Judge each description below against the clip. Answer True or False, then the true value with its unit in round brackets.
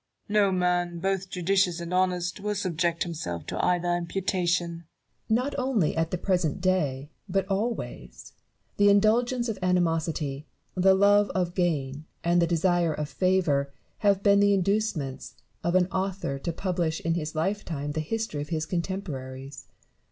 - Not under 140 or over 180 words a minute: True (150 wpm)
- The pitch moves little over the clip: False (3.3 semitones)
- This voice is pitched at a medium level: True (180 Hz)